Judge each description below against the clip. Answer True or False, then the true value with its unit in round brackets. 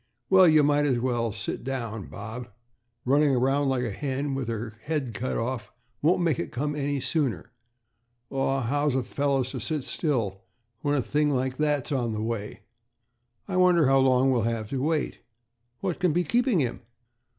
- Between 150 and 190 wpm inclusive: True (180 wpm)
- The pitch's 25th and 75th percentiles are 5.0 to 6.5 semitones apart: False (3.7 semitones)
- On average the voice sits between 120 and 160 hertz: True (135 Hz)